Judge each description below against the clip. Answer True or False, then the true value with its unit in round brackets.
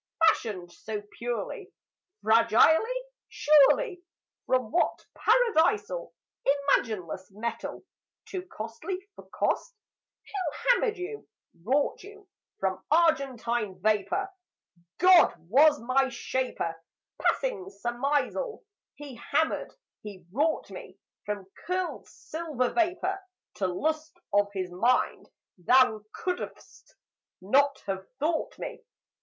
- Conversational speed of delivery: False (100 wpm)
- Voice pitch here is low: False (280 Hz)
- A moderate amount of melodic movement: False (8.8 semitones)